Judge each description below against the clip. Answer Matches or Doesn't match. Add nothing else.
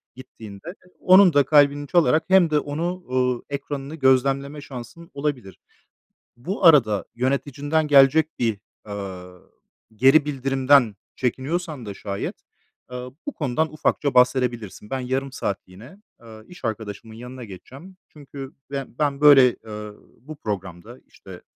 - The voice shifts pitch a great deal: Doesn't match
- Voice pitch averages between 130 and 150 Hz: Matches